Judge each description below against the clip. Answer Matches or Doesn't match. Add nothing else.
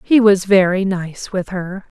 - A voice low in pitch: Doesn't match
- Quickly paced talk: Doesn't match